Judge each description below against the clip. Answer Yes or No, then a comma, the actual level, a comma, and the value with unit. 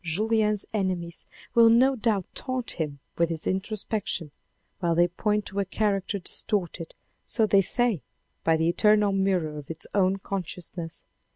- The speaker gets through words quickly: No, average, 155 wpm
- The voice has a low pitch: No, high, 195 Hz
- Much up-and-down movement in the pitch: No, average, 3.8 semitones